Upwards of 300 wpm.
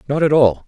No: fast, 265 wpm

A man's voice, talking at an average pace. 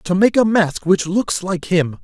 No: male; fast, 235 wpm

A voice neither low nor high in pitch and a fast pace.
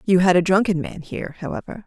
Yes: medium, 175 Hz; fast, 225 wpm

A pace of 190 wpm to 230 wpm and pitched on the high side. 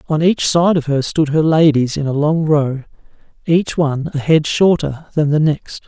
No: fast, 205 wpm; medium, 150 Hz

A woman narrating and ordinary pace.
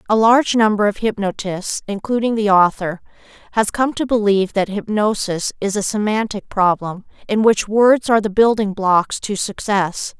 Yes: female; average, 160 wpm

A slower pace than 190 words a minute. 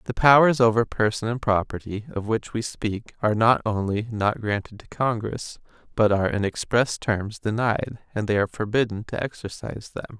Yes: average, 175 wpm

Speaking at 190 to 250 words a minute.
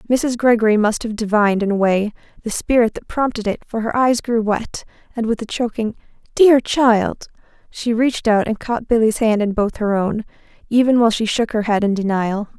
Yes: average, 200 wpm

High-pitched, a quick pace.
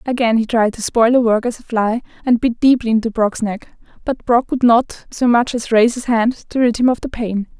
Yes: high, 235 Hz; fast, 255 wpm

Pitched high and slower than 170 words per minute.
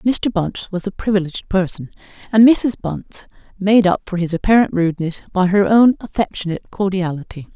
Yes: high, 195 Hz; average, 160 wpm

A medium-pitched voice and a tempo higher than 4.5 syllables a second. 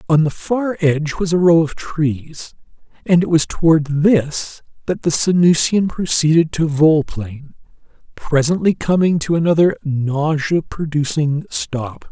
No: medium, 160 Hz; 4.1 syllables/s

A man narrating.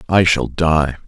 Yes: male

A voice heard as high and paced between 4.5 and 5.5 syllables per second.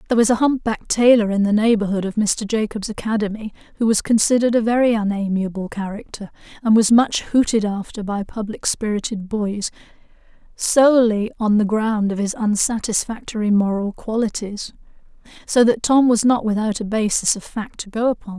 Yes: high, 215 Hz; 5.4 syllables/s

